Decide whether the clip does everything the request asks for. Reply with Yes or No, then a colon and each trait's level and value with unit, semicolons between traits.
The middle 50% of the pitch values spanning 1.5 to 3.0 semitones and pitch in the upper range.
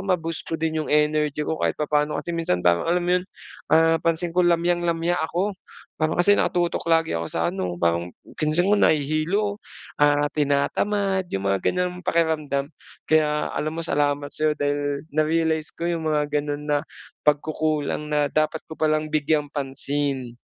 No: narrow, 2.4 semitones; medium, 155 Hz